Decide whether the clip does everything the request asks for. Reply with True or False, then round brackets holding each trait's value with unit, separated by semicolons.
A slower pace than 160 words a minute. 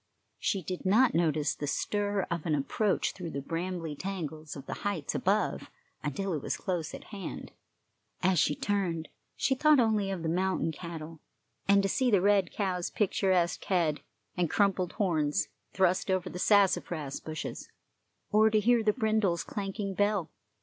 False (165 wpm)